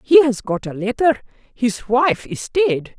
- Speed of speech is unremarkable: Yes, average, 180 wpm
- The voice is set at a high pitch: Yes, very high, 250 Hz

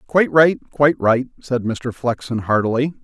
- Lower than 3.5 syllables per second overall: No, 4.9 syllables/s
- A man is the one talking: Yes, male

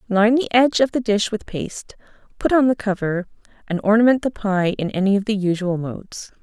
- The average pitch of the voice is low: No, high, 210 Hz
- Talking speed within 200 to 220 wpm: Yes, fast, 205 wpm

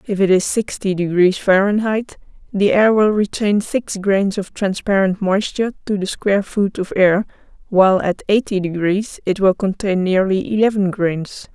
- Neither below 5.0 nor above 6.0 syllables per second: No, 4.6 syllables/s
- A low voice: No, high, 195 Hz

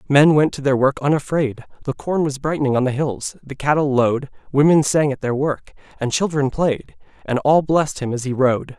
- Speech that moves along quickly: Yes, fast, 210 wpm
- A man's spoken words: Yes, male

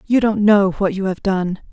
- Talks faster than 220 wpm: Yes, fast, 245 wpm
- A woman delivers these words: Yes, female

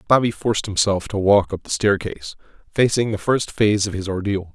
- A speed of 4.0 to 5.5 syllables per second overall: No, 5.8 syllables/s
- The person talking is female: No, male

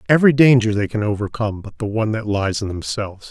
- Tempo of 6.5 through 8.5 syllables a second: Yes, 6.7 syllables/s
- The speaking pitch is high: No, low, 110 Hz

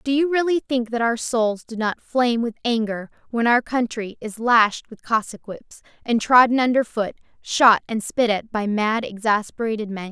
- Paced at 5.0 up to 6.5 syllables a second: No, 4.7 syllables/s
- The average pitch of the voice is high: Yes, high, 230 Hz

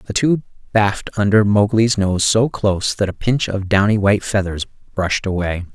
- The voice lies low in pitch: Yes, low, 105 Hz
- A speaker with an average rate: Yes, average, 180 wpm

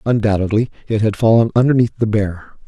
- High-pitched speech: No, low, 110 Hz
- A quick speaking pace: No, average, 155 wpm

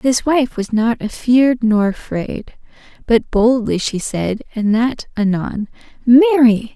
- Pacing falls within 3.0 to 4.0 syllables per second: Yes, 3.9 syllables/s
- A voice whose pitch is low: No, high, 235 Hz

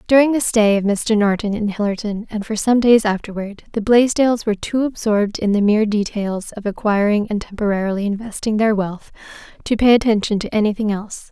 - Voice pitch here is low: No, high, 215 Hz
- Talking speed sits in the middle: Yes, average, 185 wpm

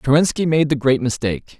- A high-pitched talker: No, medium, 140 Hz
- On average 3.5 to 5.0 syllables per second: No, 6.0 syllables/s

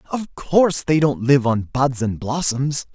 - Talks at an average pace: Yes, average, 185 wpm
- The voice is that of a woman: No, male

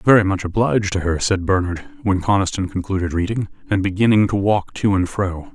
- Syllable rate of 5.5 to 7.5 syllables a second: Yes, 5.6 syllables/s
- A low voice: Yes, very low, 95 Hz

